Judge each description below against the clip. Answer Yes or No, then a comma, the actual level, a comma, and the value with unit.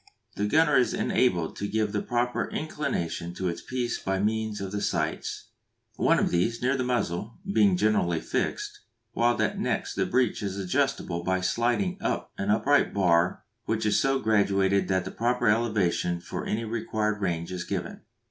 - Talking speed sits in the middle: Yes, average, 175 wpm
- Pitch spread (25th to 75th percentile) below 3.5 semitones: No, average, 4.4 semitones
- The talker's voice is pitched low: Yes, low, 105 Hz